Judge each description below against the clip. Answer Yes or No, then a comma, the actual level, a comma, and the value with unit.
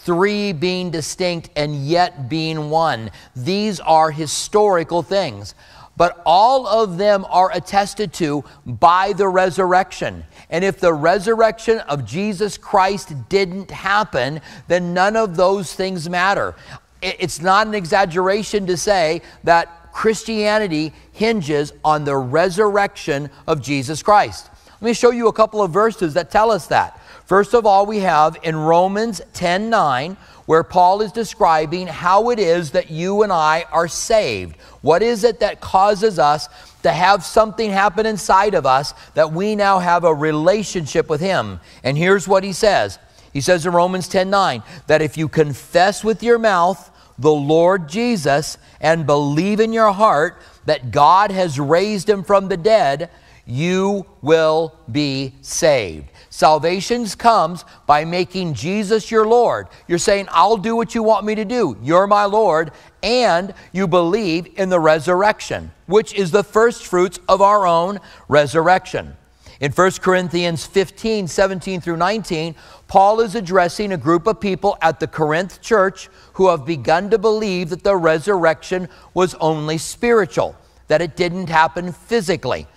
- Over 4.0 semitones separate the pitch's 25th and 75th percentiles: Yes, average, 4.4 semitones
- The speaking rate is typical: Yes, average, 155 wpm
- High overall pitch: No, medium, 180 Hz